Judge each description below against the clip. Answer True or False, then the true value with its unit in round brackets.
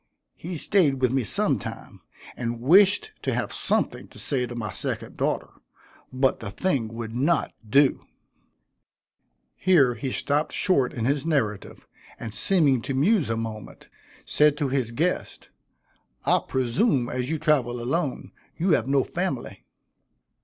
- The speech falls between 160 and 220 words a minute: False (145 wpm)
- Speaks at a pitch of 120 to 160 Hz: True (135 Hz)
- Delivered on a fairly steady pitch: False (4.9 semitones)